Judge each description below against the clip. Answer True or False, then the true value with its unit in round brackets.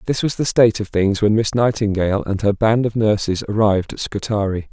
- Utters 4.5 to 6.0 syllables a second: True (5.8 syllables/s)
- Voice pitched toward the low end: True (105 Hz)